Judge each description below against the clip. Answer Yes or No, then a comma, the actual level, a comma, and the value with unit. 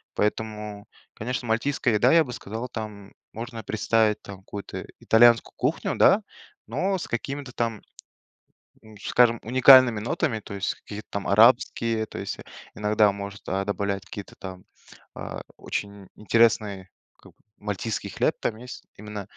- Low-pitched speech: Yes, low, 110 Hz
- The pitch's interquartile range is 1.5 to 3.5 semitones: Yes, average, 2.7 semitones